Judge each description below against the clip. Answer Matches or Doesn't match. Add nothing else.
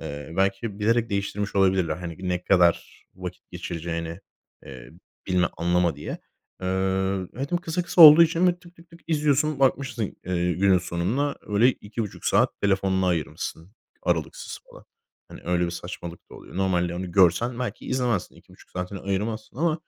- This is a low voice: Matches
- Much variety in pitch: Matches